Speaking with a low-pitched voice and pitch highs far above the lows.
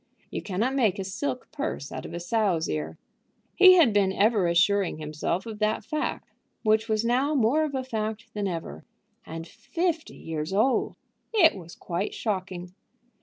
No: high, 210 Hz; wide, 6.4 semitones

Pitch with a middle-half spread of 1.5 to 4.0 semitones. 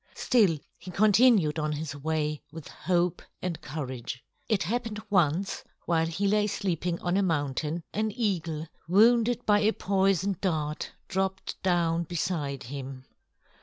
No: average, 4.6 semitones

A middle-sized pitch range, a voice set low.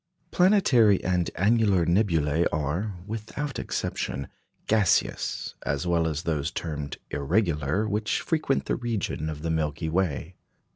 No: wide, 5.8 semitones; very low, 85 Hz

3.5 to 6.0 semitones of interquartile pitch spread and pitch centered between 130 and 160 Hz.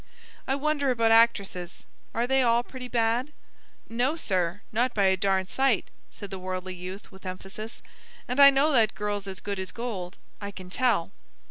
No: average, 4.7 semitones; high, 215 Hz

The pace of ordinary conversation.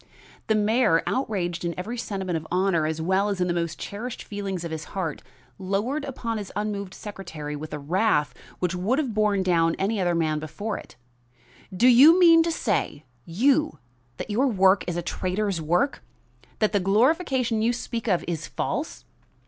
Yes: average, 180 wpm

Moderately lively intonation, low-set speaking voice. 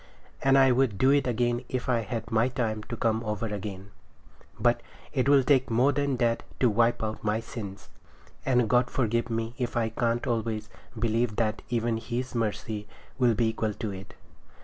No: narrow, 2.2 semitones; low, 115 Hz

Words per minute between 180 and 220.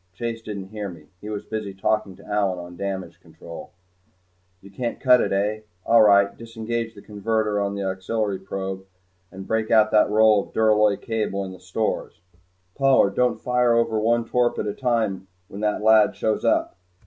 Yes: average, 185 wpm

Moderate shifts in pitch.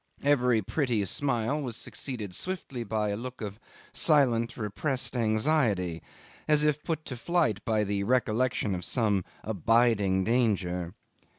Yes: average, 4.4 semitones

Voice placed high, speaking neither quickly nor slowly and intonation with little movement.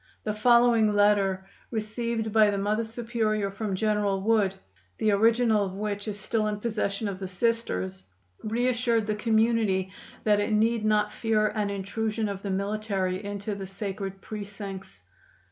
Yes: high, 210 Hz; average, 150 wpm; narrow, 1.9 semitones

